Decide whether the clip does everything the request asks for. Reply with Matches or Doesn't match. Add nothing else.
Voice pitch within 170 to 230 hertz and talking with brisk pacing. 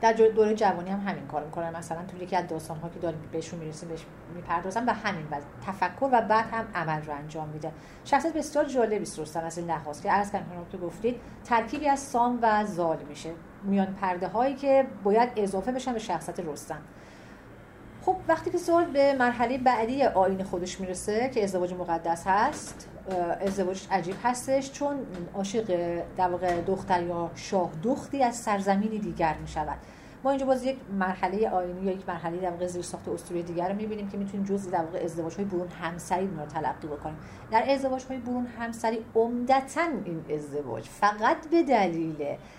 Matches